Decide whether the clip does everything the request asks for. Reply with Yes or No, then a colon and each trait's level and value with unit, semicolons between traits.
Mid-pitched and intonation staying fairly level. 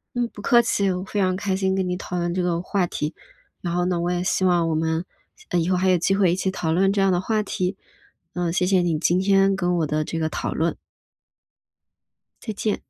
Yes: medium, 180 Hz; narrow, 2.0 semitones